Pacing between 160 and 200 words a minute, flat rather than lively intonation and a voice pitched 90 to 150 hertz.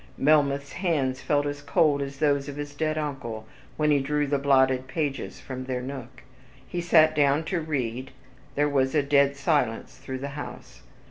Yes: average, 180 wpm; narrow, 2.0 semitones; medium, 140 Hz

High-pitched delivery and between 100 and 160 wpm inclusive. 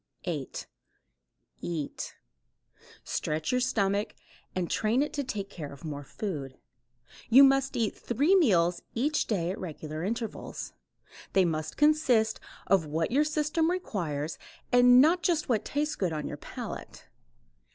Yes: high, 215 Hz; average, 140 wpm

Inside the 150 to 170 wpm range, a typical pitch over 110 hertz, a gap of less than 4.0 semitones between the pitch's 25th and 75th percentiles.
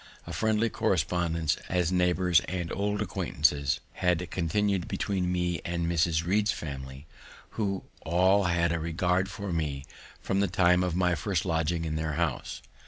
No: average, 155 wpm; very low, 90 Hz; narrow, 2.5 semitones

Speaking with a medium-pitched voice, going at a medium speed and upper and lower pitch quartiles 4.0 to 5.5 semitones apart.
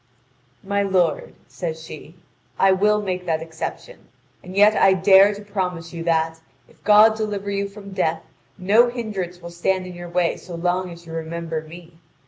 No: medium, 180 Hz; average, 175 wpm; average, 3.1 semitones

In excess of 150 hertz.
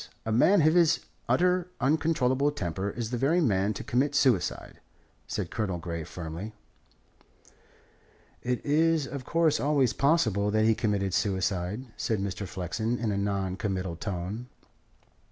No: low, 110 Hz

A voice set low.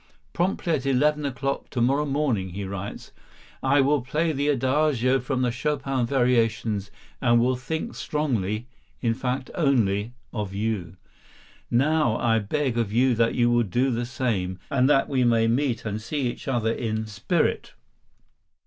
Yes: low, 125 Hz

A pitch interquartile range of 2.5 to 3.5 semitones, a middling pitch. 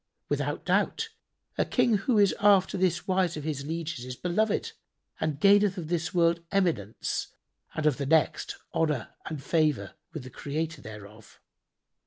No: average, 4.8 semitones; medium, 165 Hz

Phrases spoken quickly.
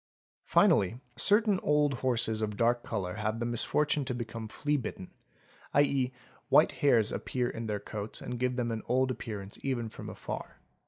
No: average, 160 wpm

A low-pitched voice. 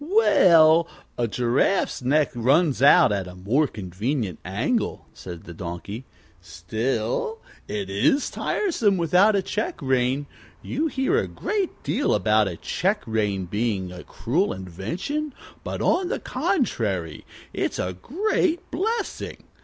Yes: low, 130 Hz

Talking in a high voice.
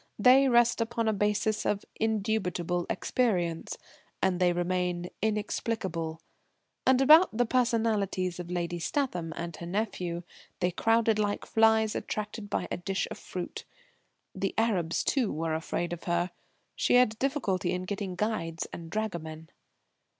Yes: high, 200 Hz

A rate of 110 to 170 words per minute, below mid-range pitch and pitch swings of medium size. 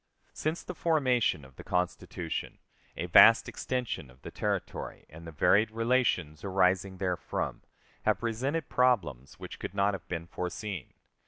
No: average, 140 wpm; low, 100 Hz; wide, 6.3 semitones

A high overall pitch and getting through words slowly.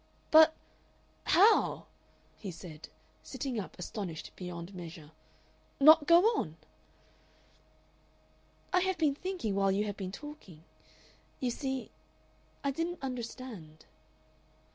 Yes: high, 235 Hz; slow, 105 wpm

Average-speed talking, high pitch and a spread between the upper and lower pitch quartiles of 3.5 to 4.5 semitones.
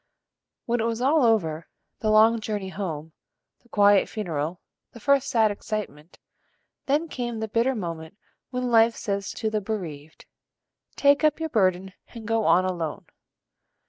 Yes: average, 150 wpm; high, 215 Hz; average, 4.2 semitones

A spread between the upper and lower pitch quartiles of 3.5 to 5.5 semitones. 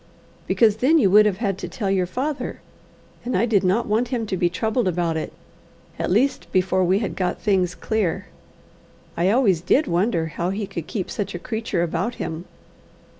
Yes: average, 4.0 semitones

